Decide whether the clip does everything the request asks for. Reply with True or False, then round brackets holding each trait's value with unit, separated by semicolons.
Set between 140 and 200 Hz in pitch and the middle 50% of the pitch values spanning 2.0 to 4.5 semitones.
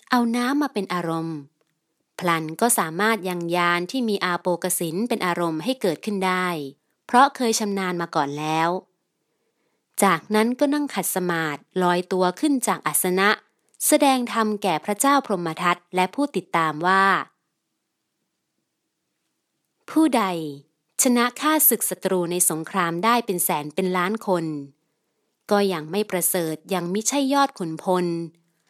False (185 Hz; 4.9 semitones)